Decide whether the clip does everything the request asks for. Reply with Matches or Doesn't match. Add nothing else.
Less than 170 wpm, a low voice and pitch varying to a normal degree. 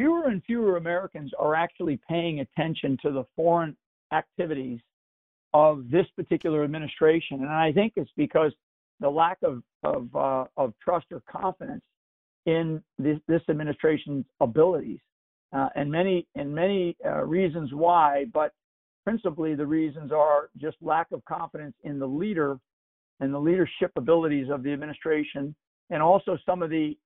Doesn't match